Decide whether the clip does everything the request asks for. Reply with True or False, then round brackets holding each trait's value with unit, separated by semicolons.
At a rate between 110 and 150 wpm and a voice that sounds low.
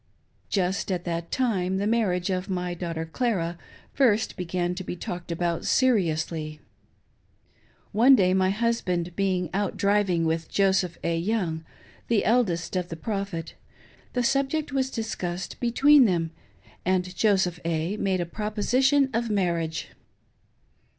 False (135 wpm; 185 Hz)